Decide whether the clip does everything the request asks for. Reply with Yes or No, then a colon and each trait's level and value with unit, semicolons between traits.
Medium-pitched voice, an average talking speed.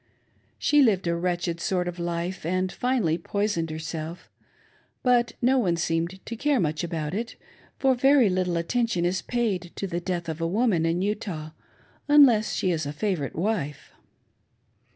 Yes: medium, 180 Hz; average, 160 wpm